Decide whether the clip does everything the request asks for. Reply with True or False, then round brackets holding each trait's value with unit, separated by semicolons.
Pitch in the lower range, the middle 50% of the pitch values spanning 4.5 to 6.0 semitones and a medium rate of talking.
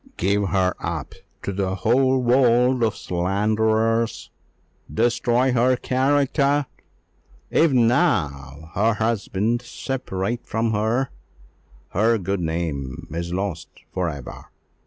False (110 Hz; 4.9 semitones; 105 wpm)